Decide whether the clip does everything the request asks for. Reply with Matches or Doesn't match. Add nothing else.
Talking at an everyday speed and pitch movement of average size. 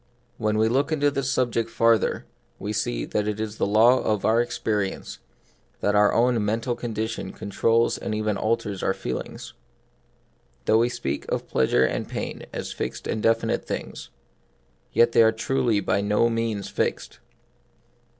Doesn't match